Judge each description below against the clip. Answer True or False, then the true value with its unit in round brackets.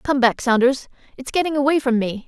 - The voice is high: True (260 Hz)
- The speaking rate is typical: False (210 wpm)